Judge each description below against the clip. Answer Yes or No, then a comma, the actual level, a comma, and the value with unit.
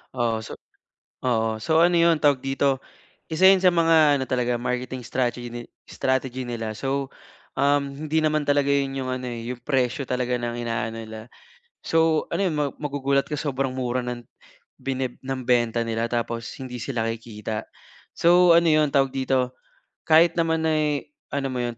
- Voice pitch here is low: Yes, low, 130 Hz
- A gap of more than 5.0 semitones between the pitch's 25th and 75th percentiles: No, average, 3.7 semitones